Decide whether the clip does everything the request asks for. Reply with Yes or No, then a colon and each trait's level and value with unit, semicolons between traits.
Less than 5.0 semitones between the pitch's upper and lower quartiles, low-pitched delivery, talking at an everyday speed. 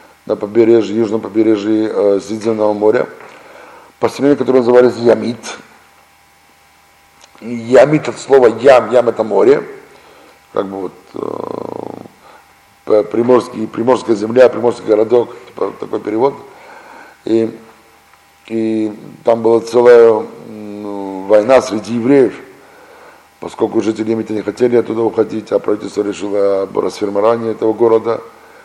No: average, 2.9 semitones; low, 115 Hz; slow, 105 wpm